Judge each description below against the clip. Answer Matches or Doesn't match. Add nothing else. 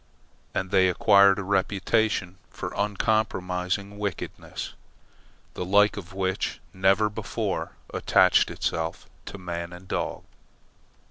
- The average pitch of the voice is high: Doesn't match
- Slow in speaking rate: Matches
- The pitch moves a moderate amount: Doesn't match